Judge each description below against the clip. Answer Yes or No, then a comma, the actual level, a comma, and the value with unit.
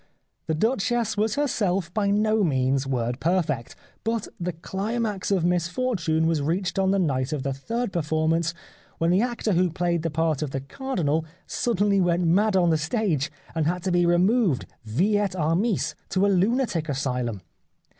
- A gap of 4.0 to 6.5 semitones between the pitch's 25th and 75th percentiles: Yes, average, 4.6 semitones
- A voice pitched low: No, medium, 175 Hz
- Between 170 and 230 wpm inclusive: Yes, average, 175 wpm